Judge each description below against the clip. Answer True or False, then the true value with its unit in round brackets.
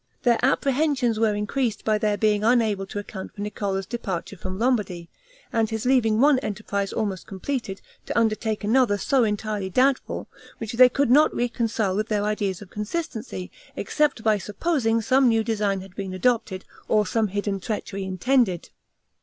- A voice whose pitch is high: True (215 Hz)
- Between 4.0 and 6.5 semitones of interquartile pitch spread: False (3.3 semitones)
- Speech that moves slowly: False (160 wpm)